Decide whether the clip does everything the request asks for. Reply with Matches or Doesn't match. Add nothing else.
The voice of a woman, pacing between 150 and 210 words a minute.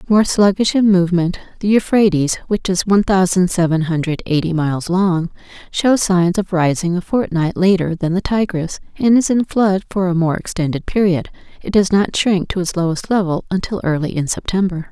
Matches